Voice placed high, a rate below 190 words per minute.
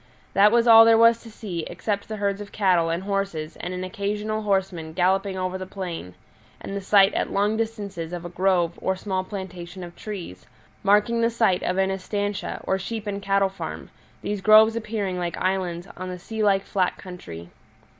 No: high, 195 Hz; average, 195 wpm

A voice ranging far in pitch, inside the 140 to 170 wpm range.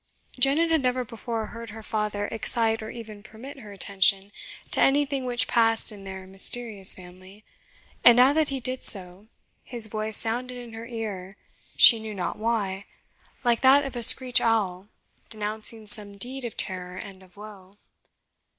No: average, 3.4 semitones; average, 165 wpm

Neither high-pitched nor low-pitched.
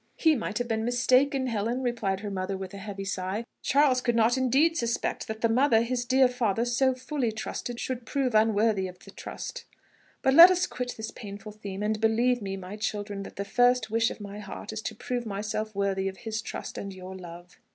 No: high, 225 Hz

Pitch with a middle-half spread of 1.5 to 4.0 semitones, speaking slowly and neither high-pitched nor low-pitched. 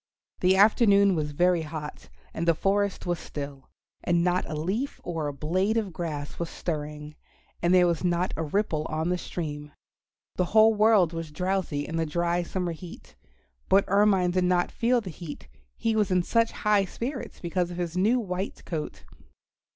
No: average, 3.6 semitones; average, 180 wpm; medium, 175 Hz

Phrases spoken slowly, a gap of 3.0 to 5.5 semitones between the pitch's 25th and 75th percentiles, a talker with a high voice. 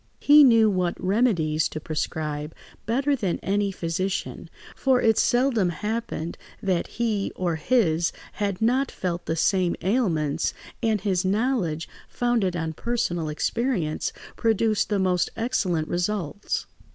Yes: slow, 125 wpm; average, 5.2 semitones; high, 195 Hz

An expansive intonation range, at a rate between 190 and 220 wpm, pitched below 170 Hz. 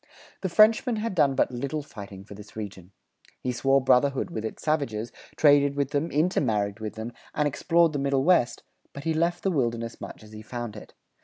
Yes: wide, 5.8 semitones; average, 200 wpm; low, 135 Hz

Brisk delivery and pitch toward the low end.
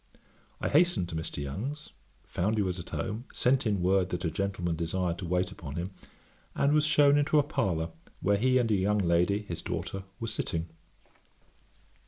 No: average, 185 wpm; very low, 95 Hz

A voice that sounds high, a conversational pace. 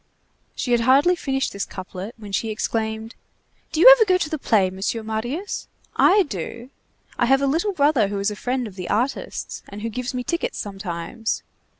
Yes: high, 235 Hz; average, 195 wpm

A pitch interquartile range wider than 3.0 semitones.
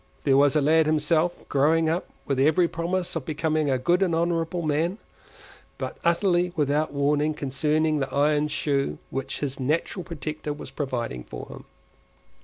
No: average, 2.7 semitones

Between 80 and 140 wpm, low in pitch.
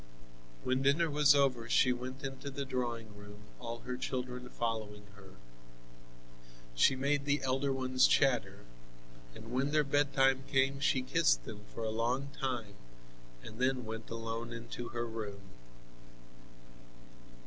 Yes: slow, 135 wpm; low, 125 Hz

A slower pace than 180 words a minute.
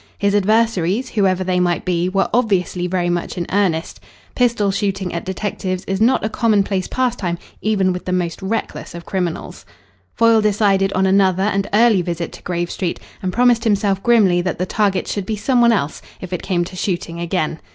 No: average, 190 wpm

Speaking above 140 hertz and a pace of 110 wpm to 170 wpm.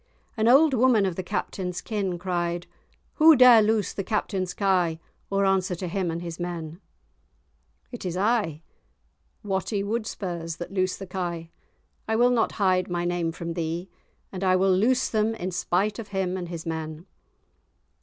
Yes: medium, 185 Hz; average, 165 wpm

